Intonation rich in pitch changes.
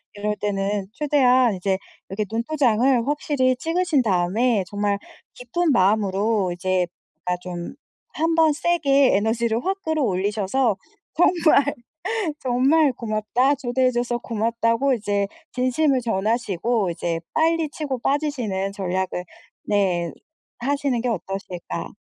Yes: wide, 5.7 semitones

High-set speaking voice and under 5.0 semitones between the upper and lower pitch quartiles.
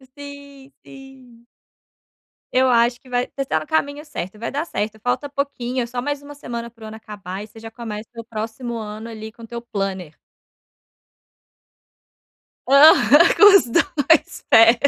Yes: high, 240 Hz; average, 4.2 semitones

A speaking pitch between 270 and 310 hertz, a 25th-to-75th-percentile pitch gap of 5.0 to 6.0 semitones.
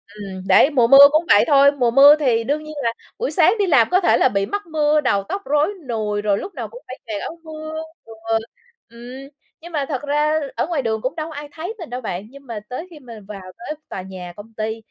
Yes: very high, 275 Hz; wide, 5.6 semitones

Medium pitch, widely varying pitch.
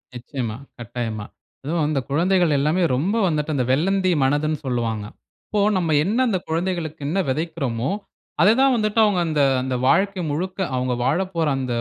Yes: medium, 155 Hz; wide, 6.1 semitones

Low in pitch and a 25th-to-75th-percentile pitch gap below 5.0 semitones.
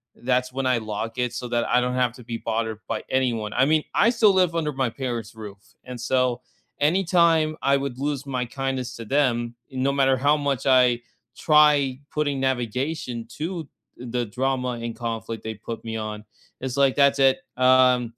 Yes: low, 130 Hz; average, 2.8 semitones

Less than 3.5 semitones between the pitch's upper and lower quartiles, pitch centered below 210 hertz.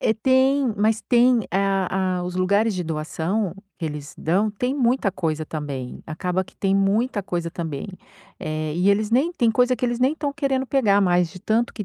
No: wide, 5.5 semitones; high, 200 Hz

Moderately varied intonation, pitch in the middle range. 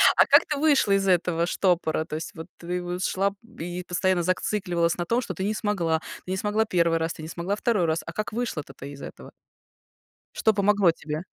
Yes: average, 3.4 semitones; medium, 180 Hz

